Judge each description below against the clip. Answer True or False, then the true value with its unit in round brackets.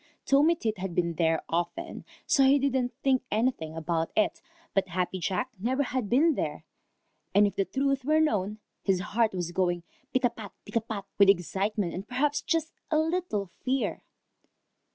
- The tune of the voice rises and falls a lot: True (6.5 semitones)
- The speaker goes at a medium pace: True (160 wpm)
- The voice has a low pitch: False (215 Hz)